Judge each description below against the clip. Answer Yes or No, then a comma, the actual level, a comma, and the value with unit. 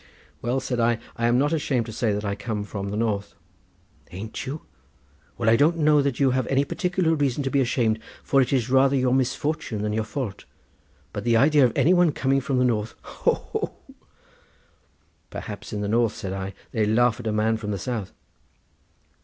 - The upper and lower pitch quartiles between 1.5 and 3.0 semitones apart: No, average, 4.2 semitones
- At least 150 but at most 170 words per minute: No, average, 200 wpm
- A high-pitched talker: No, low, 120 Hz